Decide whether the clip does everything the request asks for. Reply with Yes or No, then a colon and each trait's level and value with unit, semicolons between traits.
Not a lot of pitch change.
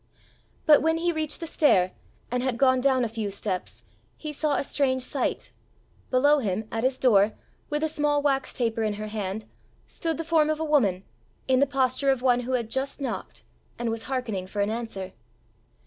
No: average, 4.7 semitones